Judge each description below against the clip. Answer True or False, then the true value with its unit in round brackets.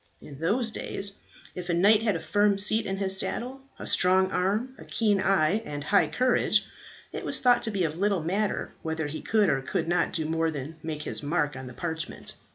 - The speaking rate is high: True (215 wpm)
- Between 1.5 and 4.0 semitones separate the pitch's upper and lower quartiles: False (4.5 semitones)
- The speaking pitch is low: False (185 Hz)